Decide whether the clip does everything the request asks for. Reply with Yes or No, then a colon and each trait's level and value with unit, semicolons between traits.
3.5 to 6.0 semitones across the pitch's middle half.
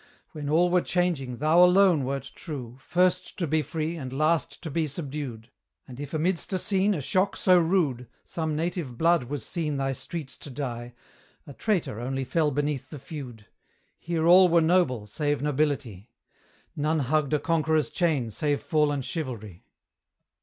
Yes: average, 4.2 semitones